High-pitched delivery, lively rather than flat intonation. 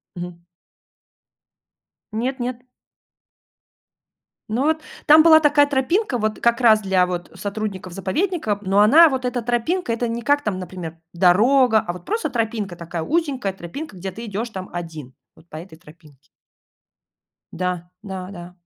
Yes: high, 215 Hz; wide, 6.3 semitones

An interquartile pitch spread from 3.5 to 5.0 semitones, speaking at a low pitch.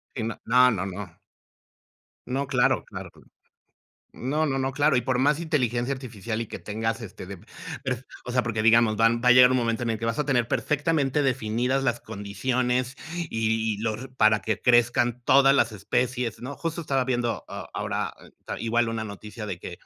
No: average, 2.8 semitones; low, 120 Hz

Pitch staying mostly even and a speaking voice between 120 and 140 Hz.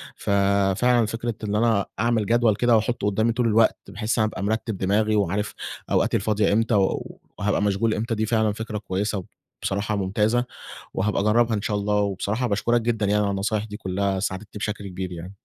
No: narrow, 1.9 semitones; low, 105 Hz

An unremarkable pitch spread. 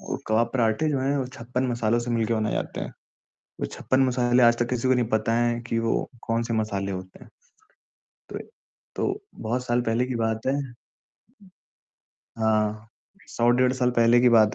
No: narrow, 1.9 semitones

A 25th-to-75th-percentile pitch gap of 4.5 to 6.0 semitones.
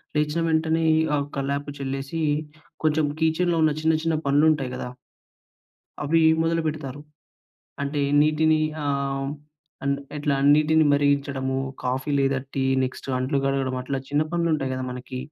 No: narrow, 2.5 semitones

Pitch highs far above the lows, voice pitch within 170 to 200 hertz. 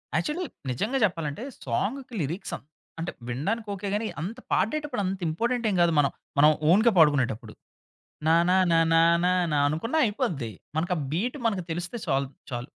Yes: wide, 7.4 semitones; medium, 180 Hz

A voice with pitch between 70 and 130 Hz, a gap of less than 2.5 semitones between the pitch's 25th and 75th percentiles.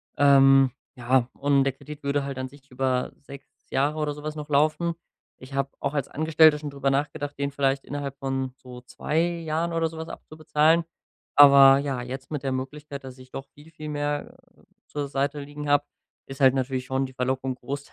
No: medium, 140 Hz; narrow, 1.9 semitones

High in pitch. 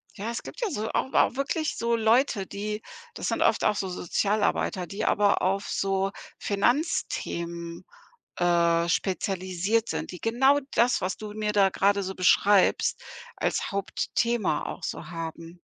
Yes: high, 200 Hz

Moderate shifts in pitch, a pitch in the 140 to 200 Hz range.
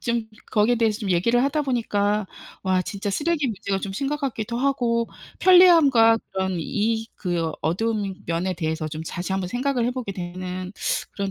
No: average, 4.8 semitones; high, 210 Hz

